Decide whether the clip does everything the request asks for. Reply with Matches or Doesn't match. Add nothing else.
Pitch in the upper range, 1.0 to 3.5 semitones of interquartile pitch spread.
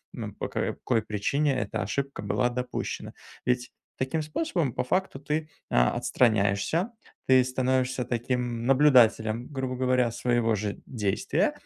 Doesn't match